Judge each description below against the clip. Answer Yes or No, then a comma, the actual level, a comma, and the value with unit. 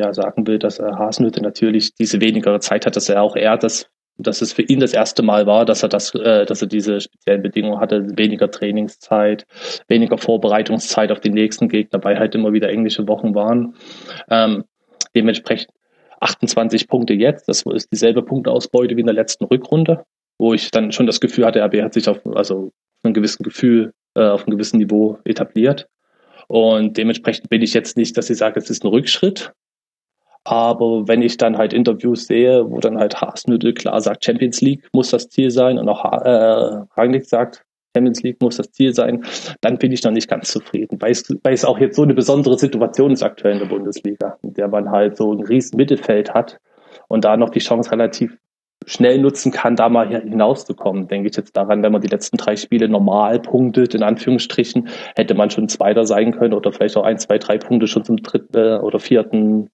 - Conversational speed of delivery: No, fast, 200 wpm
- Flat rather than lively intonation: Yes, narrow, 1.9 semitones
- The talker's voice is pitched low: Yes, low, 110 Hz